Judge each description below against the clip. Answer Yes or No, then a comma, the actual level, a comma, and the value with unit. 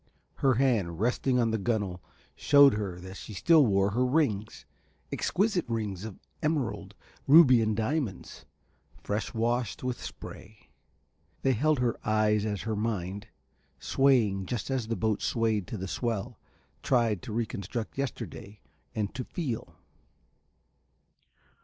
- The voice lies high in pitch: No, low, 115 Hz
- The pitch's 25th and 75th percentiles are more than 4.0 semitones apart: No, average, 3.7 semitones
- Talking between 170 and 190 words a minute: No, slow, 135 wpm